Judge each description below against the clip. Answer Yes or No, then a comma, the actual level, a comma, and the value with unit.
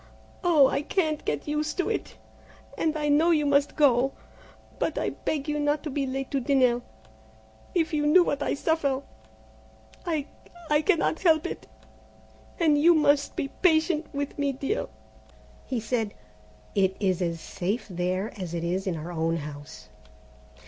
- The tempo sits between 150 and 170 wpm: Yes, average, 160 wpm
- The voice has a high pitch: Yes, very high, 285 Hz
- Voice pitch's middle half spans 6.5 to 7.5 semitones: Yes, wide, 7.0 semitones